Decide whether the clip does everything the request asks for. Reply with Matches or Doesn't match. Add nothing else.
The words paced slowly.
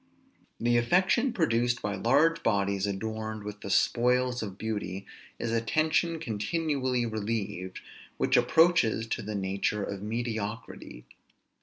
Matches